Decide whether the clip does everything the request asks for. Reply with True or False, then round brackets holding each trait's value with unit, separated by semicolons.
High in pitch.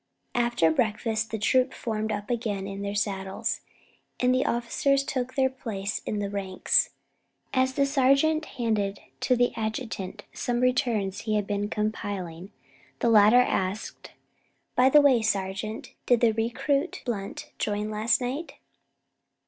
True (220 Hz)